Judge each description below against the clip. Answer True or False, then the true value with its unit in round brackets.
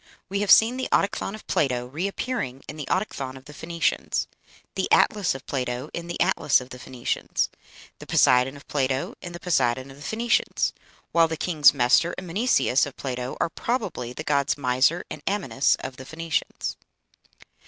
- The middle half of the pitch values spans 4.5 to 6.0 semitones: True (5.5 semitones)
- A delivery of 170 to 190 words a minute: True (175 wpm)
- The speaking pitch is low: False (145 Hz)